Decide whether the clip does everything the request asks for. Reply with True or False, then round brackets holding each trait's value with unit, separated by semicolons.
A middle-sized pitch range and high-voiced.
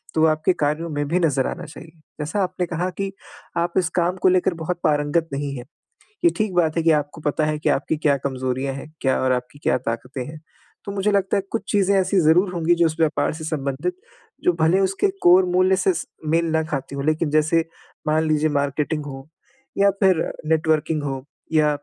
False (3.5 semitones; 160 Hz)